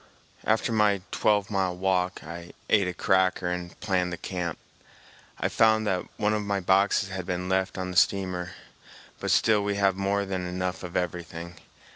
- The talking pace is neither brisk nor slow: Yes, average, 175 wpm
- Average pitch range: No, narrow, 2.1 semitones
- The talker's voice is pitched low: Yes, very low, 95 Hz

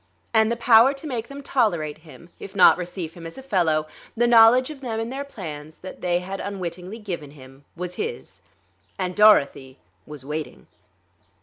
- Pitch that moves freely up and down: Yes, wide, 6.5 semitones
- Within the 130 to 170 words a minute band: No, average, 180 wpm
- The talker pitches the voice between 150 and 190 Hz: Yes, medium, 185 Hz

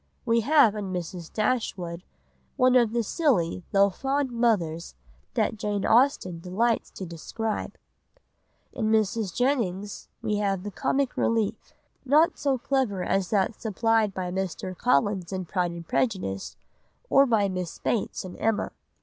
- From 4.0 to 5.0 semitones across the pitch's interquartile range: Yes, average, 4.3 semitones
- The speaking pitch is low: No, high, 205 Hz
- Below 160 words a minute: Yes, average, 140 wpm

